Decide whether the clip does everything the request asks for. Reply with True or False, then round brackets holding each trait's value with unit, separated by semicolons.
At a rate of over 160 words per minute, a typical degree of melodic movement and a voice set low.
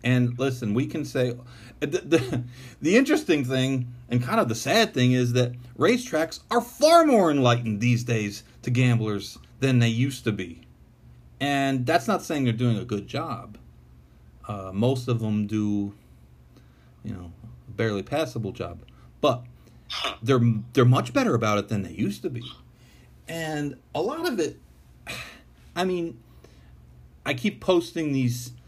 False (155 wpm; 4.5 semitones; 120 Hz)